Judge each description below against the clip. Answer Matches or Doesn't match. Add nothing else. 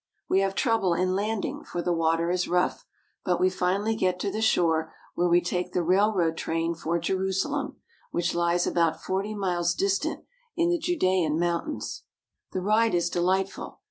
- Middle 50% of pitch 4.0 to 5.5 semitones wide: Doesn't match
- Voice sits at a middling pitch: Matches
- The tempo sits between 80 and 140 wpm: Doesn't match